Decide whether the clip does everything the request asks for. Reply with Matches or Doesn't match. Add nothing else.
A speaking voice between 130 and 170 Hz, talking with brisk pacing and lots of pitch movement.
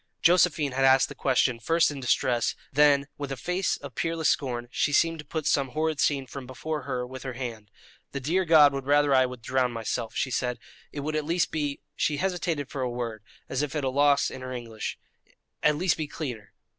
Doesn't match